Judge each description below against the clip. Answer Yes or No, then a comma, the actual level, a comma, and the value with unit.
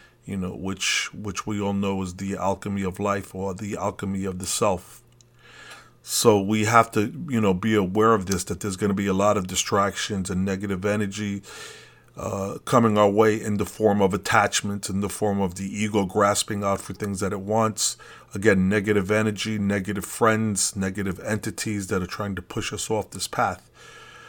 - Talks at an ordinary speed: Yes, average, 195 wpm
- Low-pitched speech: Yes, low, 100 Hz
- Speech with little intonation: Yes, narrow, 1.7 semitones